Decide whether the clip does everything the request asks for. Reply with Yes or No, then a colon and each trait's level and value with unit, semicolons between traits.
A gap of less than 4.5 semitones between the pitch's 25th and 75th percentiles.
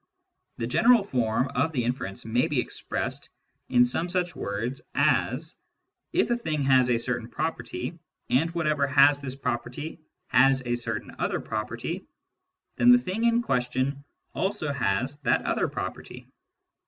No: average, 4.9 semitones